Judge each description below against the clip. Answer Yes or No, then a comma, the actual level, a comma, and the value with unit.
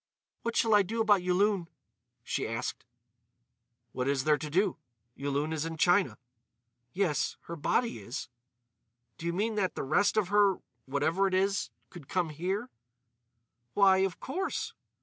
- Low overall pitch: No, medium, 180 Hz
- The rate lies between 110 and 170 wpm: Yes, average, 145 wpm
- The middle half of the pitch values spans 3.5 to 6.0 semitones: Yes, average, 5.1 semitones